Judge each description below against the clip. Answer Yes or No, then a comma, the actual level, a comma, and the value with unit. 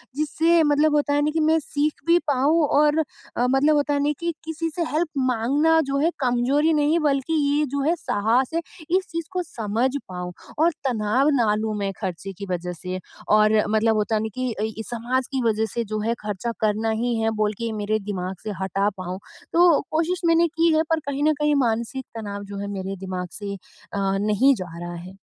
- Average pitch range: No, wide, 6.4 semitones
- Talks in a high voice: Yes, high, 245 Hz